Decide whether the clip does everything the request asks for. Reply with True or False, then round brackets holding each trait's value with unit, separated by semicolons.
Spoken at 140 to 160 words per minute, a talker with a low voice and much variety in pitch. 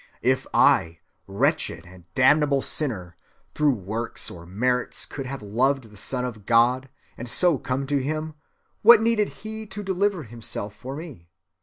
True (155 wpm; 130 Hz; 6.1 semitones)